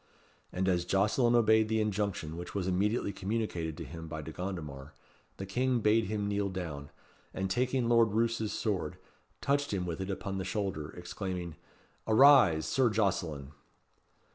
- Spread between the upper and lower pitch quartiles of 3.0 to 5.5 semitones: Yes, average, 4.1 semitones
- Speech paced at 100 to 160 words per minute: Yes, average, 155 wpm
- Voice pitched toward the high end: No, low, 100 Hz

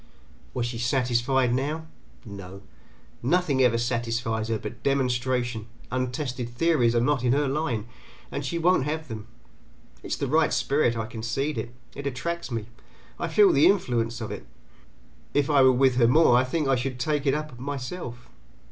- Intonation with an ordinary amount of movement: Yes, average, 3.3 semitones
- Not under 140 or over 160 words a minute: No, average, 175 wpm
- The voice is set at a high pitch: No, low, 125 Hz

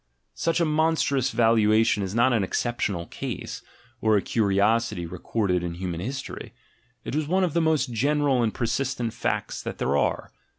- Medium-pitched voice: No, low, 115 Hz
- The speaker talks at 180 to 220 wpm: No, average, 165 wpm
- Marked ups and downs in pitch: Yes, wide, 5.7 semitones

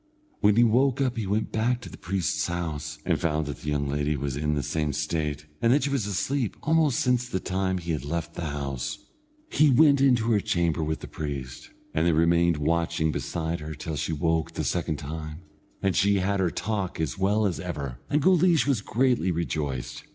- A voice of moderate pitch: No, very low, 85 Hz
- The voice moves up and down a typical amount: No, wide, 6.4 semitones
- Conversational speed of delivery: No, fast, 210 wpm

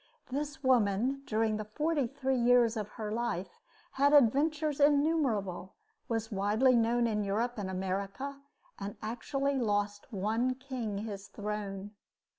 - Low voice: No, high, 230 Hz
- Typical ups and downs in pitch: Yes, average, 4.7 semitones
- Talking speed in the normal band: No, slow, 130 wpm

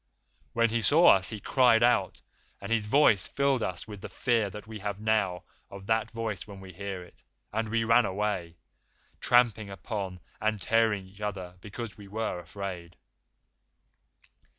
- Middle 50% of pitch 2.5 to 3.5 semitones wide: Yes, average, 2.8 semitones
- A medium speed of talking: Yes, average, 165 wpm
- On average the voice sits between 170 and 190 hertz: No, low, 105 Hz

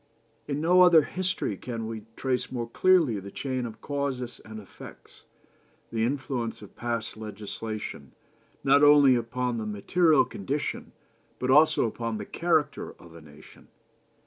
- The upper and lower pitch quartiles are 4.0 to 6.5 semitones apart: Yes, average, 4.6 semitones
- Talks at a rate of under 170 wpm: Yes, average, 145 wpm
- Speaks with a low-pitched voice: Yes, low, 125 Hz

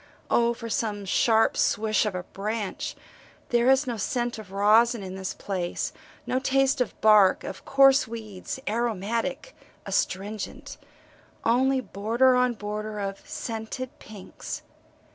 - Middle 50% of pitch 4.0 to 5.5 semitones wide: No, average, 3.1 semitones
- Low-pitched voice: No, high, 220 Hz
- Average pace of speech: No, slow, 130 wpm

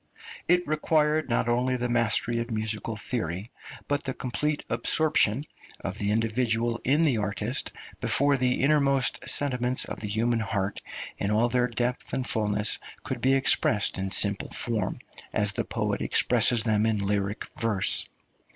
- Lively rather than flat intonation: No, average, 3.5 semitones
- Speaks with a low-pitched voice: Yes, low, 120 Hz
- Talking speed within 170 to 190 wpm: No, average, 150 wpm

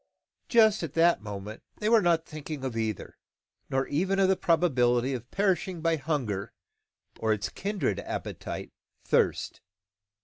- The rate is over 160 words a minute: No, average, 140 wpm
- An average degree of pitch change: No, wide, 7.4 semitones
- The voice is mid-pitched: Yes, medium, 155 Hz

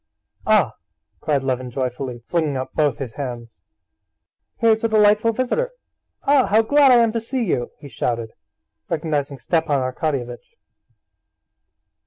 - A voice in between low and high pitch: Yes, medium, 150 Hz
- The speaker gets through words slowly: Yes, slow, 130 wpm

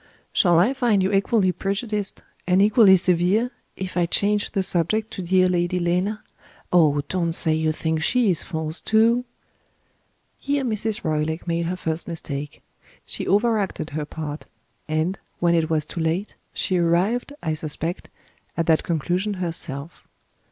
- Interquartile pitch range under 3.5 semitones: No, average, 4.1 semitones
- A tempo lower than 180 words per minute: Yes, average, 155 wpm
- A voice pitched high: No, medium, 180 Hz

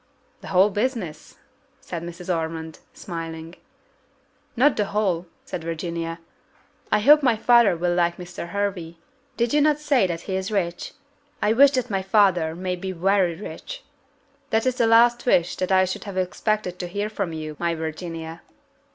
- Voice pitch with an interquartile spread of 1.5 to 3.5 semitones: No, average, 4.1 semitones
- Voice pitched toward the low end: No, medium, 185 Hz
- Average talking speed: Yes, average, 170 wpm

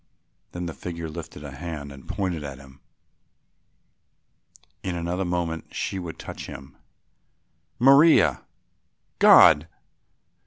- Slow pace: Yes, slow, 110 wpm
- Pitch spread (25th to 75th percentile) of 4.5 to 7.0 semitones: No, average, 3.6 semitones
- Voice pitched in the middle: No, very low, 85 Hz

